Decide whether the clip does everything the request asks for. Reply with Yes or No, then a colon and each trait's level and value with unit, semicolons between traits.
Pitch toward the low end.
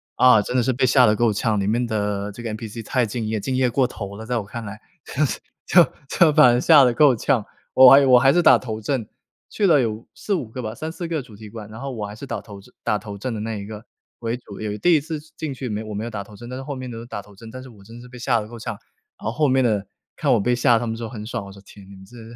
Yes: low, 115 Hz